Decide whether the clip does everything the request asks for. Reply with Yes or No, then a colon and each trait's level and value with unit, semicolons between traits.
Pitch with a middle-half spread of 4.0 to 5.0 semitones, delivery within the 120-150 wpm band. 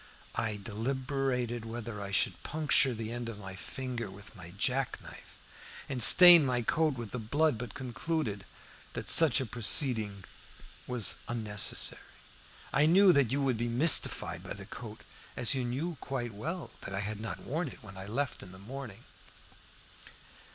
No: average, 4.3 semitones; average, 170 wpm